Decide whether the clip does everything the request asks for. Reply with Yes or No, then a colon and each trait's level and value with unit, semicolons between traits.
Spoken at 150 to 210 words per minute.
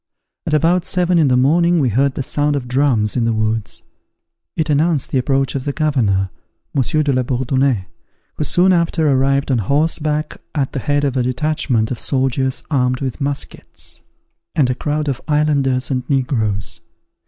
Yes: average, 175 wpm